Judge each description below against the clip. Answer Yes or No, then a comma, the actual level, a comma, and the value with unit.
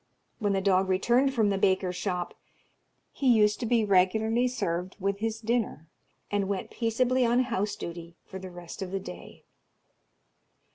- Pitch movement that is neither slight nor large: Yes, average, 3.6 semitones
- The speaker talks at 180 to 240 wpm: No, average, 160 wpm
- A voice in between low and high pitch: No, high, 200 Hz